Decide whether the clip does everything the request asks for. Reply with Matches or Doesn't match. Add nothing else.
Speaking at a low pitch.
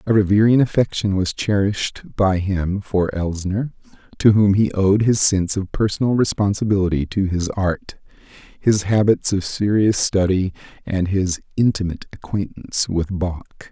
Matches